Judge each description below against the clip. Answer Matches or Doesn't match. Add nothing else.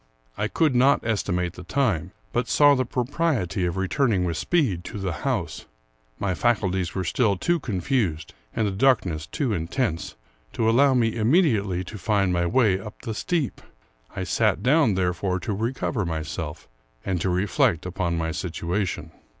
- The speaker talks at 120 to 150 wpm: Doesn't match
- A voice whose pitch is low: Matches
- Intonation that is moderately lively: Doesn't match